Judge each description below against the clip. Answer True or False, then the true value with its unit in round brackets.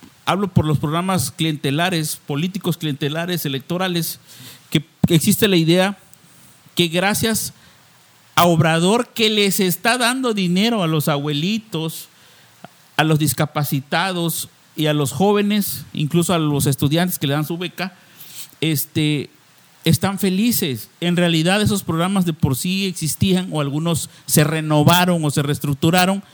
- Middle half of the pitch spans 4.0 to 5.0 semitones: False (3.3 semitones)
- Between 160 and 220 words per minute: False (130 wpm)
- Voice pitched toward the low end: False (165 Hz)